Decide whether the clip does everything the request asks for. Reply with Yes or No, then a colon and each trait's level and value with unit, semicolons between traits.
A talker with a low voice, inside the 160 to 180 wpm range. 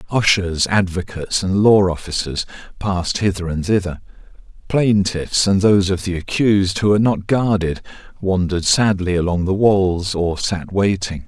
No: very low, 95 Hz; average, 145 wpm